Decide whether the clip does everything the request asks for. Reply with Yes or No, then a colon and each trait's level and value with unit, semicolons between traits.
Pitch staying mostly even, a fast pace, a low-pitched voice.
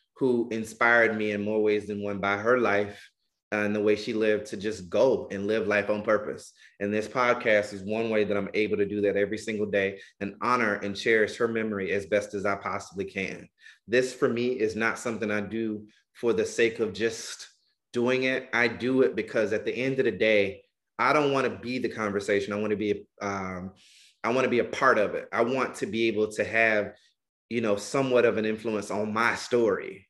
Yes: narrow, 2.3 semitones; fast, 225 wpm; low, 105 Hz